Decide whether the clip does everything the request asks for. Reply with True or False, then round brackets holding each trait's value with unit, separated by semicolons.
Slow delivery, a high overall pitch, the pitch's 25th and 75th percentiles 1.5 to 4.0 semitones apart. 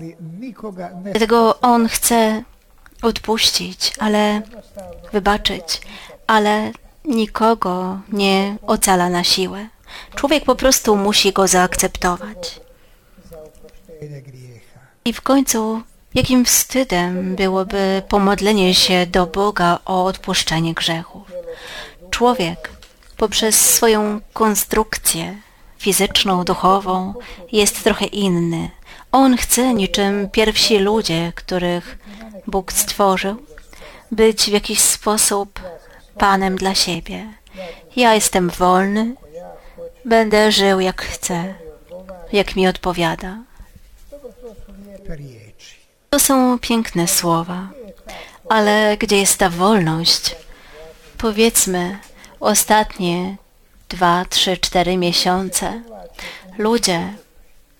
True (85 wpm; 195 Hz; 3.4 semitones)